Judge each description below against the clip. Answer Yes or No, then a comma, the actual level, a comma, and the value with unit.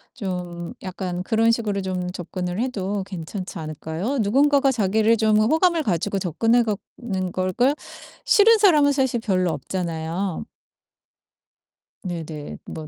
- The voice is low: No, high, 195 Hz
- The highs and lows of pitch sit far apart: No, average, 4.6 semitones